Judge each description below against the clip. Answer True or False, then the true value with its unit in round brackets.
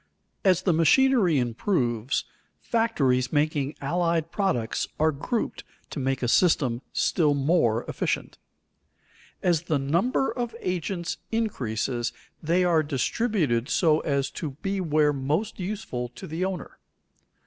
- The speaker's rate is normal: False (125 wpm)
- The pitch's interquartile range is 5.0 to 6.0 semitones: True (5.4 semitones)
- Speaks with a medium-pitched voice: True (155 Hz)